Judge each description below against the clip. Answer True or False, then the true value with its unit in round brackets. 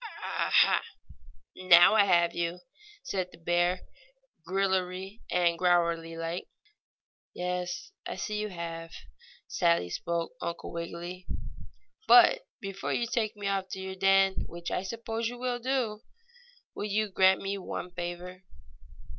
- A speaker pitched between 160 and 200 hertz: True (185 Hz)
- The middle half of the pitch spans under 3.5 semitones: True (2.4 semitones)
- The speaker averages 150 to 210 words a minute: False (135 wpm)